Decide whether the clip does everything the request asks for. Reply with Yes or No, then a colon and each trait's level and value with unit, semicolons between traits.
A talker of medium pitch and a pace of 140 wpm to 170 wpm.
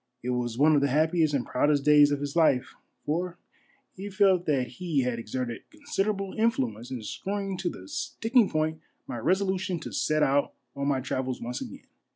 No: medium, 150 Hz; average, 185 wpm